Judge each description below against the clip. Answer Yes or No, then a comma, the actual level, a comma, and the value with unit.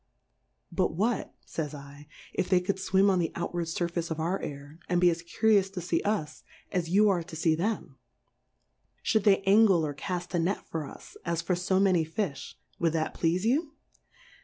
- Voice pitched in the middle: Yes, medium, 175 Hz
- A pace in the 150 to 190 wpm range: No, average, 200 wpm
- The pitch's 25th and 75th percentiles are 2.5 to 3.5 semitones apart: Yes, average, 2.9 semitones